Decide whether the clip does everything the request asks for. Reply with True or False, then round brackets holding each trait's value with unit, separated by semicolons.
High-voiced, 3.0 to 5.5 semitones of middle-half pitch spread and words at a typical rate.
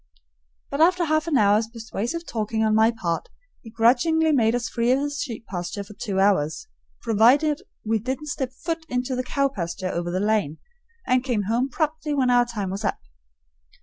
True (235 Hz; 4.9 semitones; 185 wpm)